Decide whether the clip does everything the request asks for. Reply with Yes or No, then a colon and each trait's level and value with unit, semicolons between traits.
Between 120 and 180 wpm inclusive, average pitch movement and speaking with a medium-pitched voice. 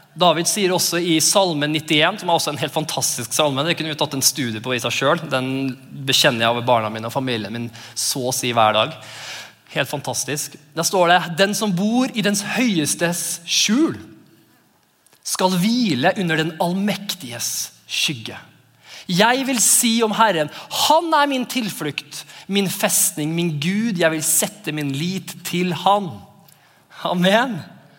No: average, 160 wpm; wide, 6.1 semitones; medium, 165 Hz